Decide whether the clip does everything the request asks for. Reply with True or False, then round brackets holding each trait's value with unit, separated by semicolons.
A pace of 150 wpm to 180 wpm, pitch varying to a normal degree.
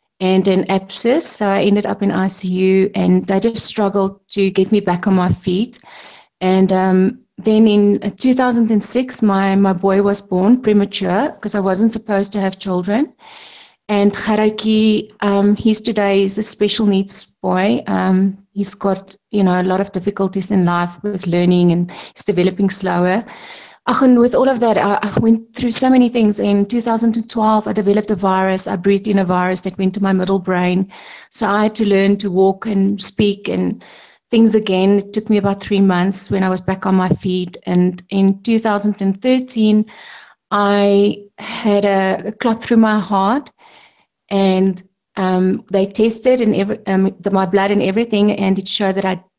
False (175 wpm; 2.1 semitones)